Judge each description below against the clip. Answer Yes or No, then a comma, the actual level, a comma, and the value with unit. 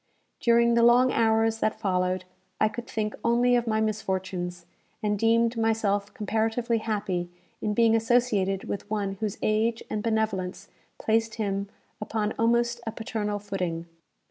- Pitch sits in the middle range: No, high, 220 Hz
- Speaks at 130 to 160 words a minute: Yes, average, 145 wpm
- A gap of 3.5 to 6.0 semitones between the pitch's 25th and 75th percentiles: No, narrow, 2.4 semitones